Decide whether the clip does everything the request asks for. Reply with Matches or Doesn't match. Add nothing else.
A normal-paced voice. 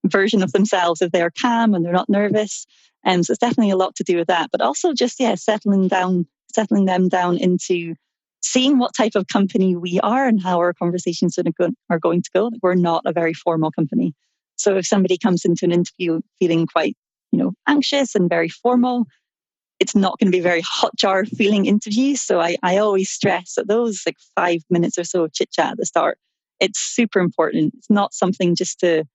Doesn't match